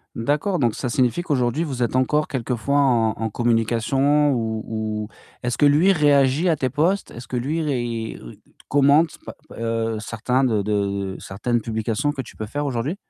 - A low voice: Yes, low, 125 Hz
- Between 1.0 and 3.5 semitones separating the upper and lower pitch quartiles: No, average, 4.2 semitones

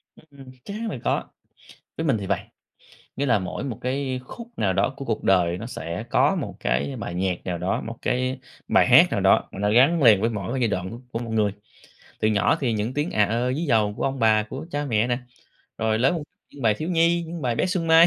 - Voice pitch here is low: Yes, low, 120 Hz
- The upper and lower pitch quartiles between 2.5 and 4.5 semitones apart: No, average, 5.2 semitones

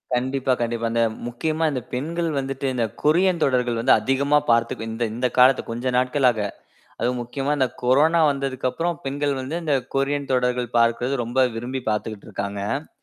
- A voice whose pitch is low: Yes, low, 130 Hz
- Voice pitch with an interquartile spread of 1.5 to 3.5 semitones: Yes, average, 2.7 semitones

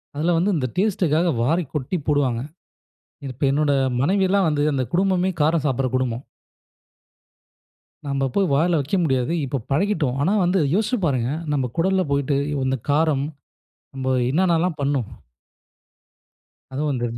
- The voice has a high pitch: No, medium, 150 Hz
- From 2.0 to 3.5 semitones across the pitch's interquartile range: No, average, 5.0 semitones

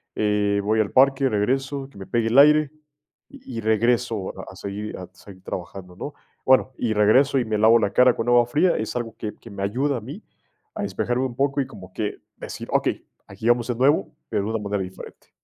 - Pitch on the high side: No, low, 115 Hz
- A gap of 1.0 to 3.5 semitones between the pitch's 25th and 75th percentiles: No, average, 4.2 semitones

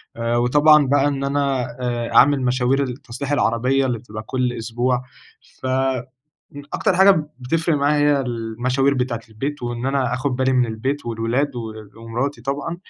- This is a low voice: Yes, low, 130 Hz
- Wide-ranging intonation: No, average, 2.7 semitones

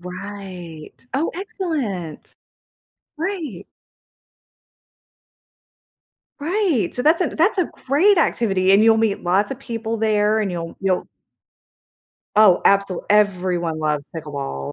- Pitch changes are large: Yes, wide, 7.4 semitones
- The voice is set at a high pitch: Yes, high, 205 Hz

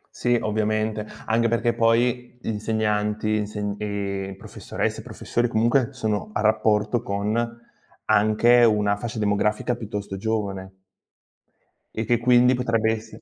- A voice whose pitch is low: Yes, low, 110 Hz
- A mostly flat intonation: Yes, narrow, 2.0 semitones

